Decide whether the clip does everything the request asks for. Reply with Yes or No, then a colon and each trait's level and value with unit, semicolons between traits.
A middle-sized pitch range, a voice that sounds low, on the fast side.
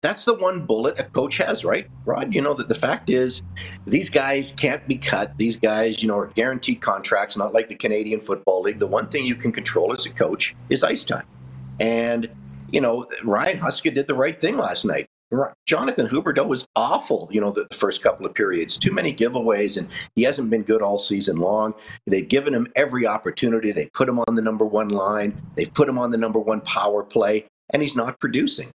Yes: average, 4.1 semitones; low, 110 Hz; fast, 215 wpm